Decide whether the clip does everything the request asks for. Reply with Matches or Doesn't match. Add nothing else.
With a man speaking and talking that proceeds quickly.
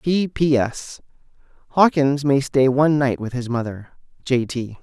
Doesn't match